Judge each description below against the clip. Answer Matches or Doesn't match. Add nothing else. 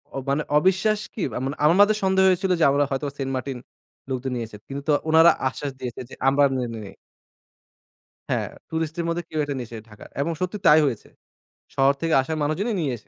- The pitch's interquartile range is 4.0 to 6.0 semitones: Matches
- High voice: Doesn't match